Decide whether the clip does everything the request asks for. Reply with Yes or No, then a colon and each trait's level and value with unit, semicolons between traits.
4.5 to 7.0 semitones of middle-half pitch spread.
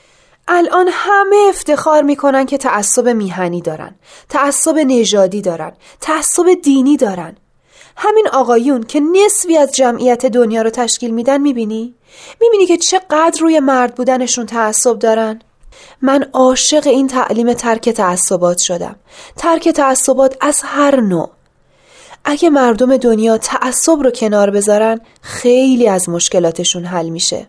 Yes: average, 5.2 semitones